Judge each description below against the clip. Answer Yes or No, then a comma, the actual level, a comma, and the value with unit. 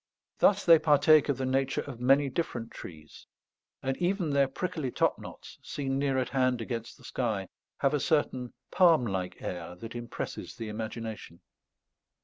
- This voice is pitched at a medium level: No, low, 130 Hz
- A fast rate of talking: No, average, 160 wpm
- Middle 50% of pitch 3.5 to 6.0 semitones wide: Yes, average, 4.1 semitones